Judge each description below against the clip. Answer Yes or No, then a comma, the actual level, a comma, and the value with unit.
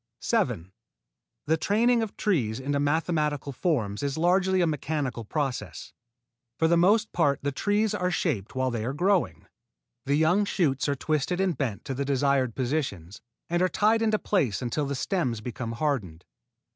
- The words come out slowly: No, average, 165 wpm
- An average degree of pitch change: No, wide, 5.8 semitones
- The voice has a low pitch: No, medium, 145 Hz